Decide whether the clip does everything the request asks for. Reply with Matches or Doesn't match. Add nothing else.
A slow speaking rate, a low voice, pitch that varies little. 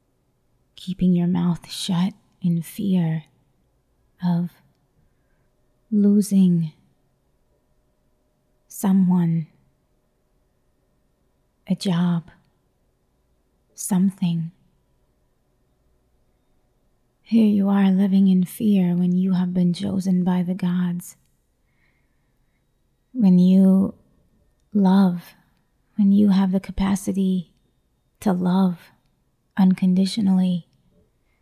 Doesn't match